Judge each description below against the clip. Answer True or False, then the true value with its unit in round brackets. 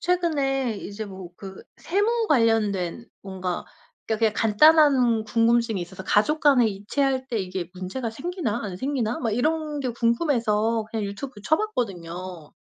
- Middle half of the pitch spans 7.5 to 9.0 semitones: False (5.5 semitones)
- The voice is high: True (230 Hz)